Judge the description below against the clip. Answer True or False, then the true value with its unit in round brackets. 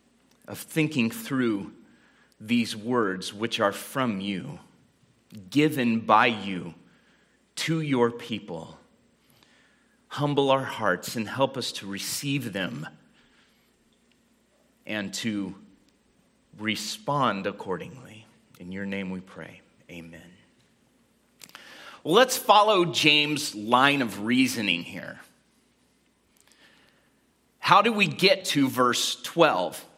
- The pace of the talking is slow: True (100 wpm)